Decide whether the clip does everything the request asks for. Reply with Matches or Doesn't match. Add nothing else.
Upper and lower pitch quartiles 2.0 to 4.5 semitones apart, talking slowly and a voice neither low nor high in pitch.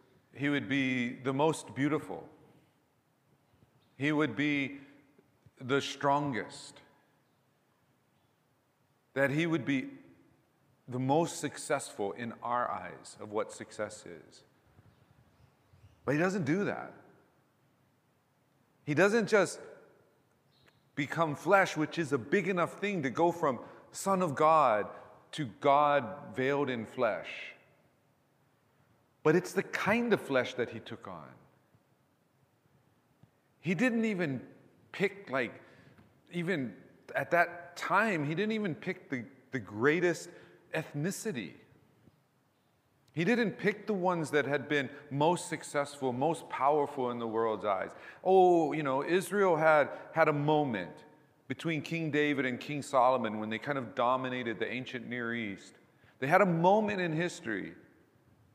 Matches